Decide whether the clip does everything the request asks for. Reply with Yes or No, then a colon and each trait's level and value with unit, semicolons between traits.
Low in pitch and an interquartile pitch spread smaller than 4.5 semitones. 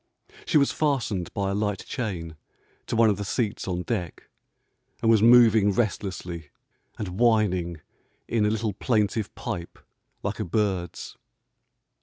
Yes: low, 105 Hz; average, 3.7 semitones